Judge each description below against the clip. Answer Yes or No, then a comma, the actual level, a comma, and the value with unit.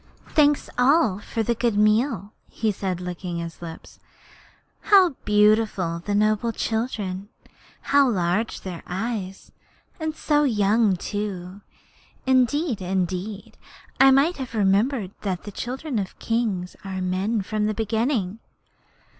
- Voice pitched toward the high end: Yes, high, 210 Hz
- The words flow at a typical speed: No, slow, 130 wpm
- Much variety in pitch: No, average, 4.0 semitones